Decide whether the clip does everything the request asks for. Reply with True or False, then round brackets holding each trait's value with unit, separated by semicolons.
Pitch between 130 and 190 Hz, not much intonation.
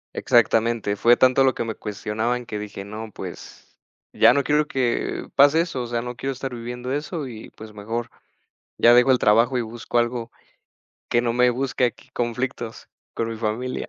False (120 Hz; 2.2 semitones)